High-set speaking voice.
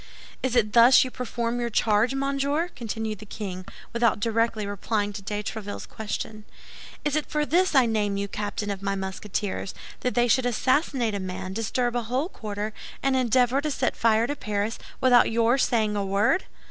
Yes: high, 225 Hz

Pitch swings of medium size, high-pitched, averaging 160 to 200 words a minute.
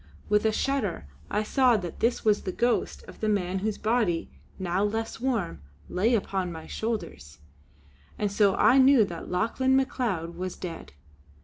Yes: average, 4.4 semitones; high, 210 Hz; average, 165 wpm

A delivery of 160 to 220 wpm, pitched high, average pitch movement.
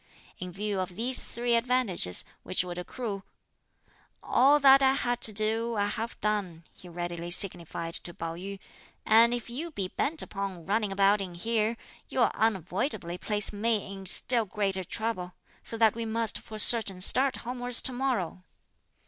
Yes: average, 165 wpm; high, 210 Hz; average, 4.2 semitones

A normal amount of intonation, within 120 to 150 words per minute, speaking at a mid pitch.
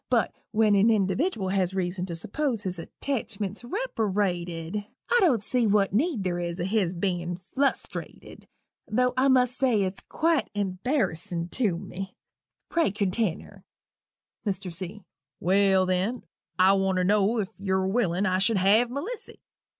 No: average, 4.0 semitones; average, 145 wpm; high, 200 Hz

